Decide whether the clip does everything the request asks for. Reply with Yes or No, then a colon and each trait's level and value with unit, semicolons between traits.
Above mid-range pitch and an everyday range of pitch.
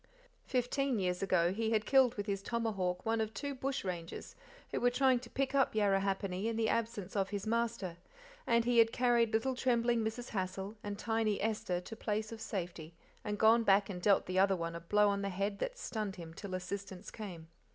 Yes: high, 210 Hz; average, 3.3 semitones